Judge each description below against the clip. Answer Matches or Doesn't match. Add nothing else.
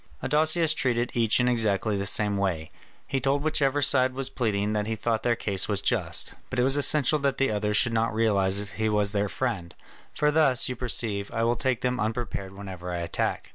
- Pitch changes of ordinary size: Matches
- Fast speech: Matches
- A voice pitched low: Matches